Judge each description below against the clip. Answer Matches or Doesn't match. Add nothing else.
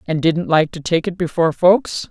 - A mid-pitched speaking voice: Matches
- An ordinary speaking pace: Doesn't match